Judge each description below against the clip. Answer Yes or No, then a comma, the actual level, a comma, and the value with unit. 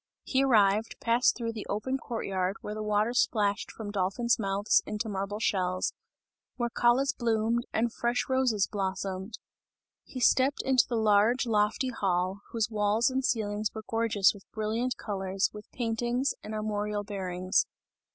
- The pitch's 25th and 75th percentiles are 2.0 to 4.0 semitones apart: Yes, average, 2.8 semitones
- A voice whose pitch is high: Yes, high, 215 Hz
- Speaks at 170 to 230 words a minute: No, average, 150 wpm